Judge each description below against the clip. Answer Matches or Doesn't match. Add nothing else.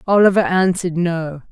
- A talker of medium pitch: Matches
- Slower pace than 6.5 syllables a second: Matches